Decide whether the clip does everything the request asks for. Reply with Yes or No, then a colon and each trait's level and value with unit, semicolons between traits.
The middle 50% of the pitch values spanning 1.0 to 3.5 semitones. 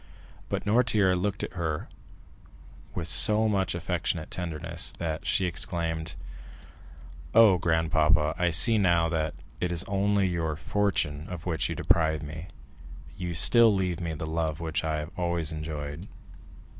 Yes: average, 2.8 semitones